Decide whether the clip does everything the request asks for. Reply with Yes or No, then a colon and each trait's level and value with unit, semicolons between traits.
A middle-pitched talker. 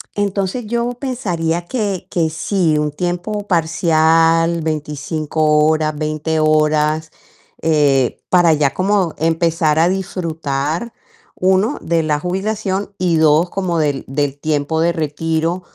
Yes: medium, 165 Hz